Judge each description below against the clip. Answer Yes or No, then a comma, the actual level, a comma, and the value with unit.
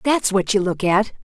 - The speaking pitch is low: No, high, 200 Hz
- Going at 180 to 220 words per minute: No, fast, 240 wpm